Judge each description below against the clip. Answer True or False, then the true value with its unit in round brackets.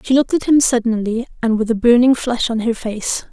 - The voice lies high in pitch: True (235 Hz)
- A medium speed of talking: False (235 wpm)